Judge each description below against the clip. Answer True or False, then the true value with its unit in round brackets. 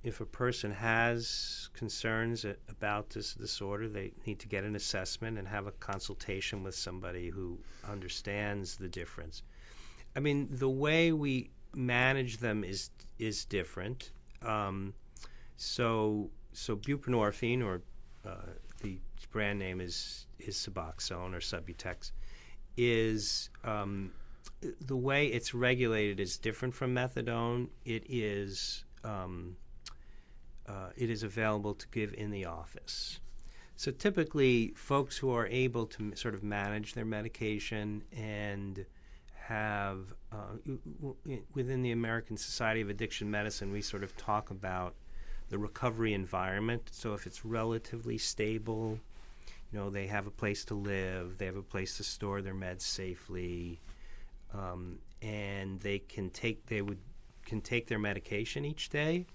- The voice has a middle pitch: False (105 Hz)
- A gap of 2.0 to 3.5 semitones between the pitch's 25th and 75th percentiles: True (3.2 semitones)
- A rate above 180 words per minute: False (140 wpm)